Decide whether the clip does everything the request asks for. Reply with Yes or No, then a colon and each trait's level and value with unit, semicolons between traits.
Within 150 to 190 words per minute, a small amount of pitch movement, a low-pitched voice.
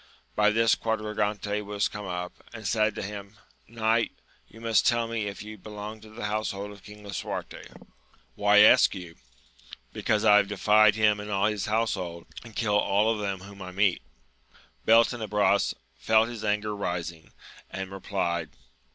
Yes: average, 175 wpm; narrow, 1.6 semitones; low, 105 Hz